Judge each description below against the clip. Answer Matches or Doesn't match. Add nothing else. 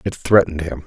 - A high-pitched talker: Doesn't match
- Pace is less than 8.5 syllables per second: Matches